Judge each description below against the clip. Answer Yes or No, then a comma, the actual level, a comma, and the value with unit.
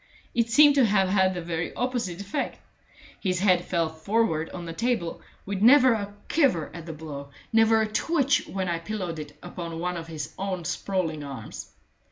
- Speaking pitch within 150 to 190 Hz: Yes, medium, 185 Hz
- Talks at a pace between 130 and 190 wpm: Yes, average, 185 wpm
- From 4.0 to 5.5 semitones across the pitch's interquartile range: Yes, average, 5.1 semitones